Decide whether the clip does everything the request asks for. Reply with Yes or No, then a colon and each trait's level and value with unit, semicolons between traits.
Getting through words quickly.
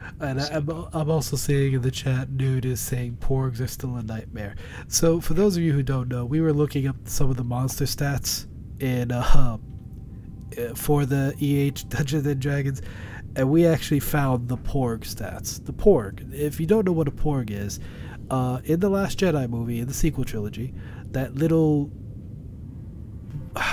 No: average, 180 wpm